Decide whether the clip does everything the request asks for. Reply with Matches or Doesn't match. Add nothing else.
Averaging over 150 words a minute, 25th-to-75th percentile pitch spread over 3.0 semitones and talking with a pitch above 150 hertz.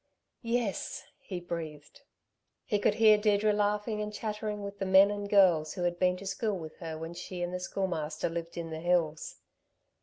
Matches